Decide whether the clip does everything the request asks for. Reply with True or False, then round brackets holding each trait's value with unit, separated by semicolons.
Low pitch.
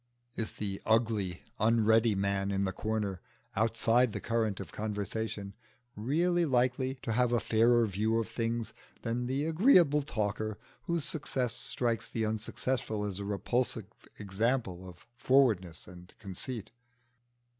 True (110 Hz)